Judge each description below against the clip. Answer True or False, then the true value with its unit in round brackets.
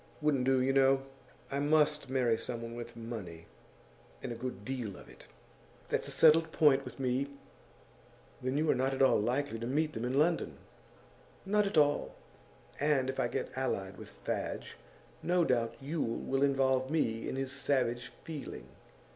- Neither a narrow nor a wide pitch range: True (3.3 semitones)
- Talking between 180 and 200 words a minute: False (170 wpm)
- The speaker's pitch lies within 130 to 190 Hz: True (135 Hz)